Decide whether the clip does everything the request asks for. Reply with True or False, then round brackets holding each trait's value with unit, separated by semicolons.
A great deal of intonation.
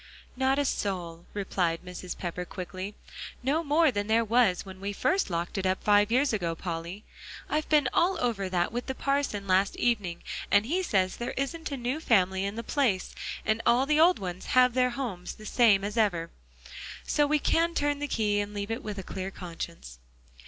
True (6.1 semitones)